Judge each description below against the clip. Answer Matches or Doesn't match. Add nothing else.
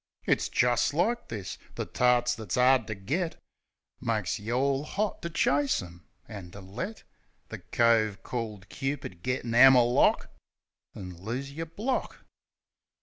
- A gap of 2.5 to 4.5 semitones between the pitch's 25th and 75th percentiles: Doesn't match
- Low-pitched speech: Matches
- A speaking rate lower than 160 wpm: Matches